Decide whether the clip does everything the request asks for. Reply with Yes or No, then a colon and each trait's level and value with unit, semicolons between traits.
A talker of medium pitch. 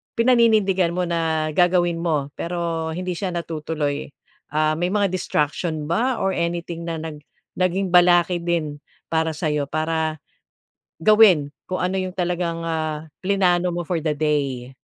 Yes: medium, 170 Hz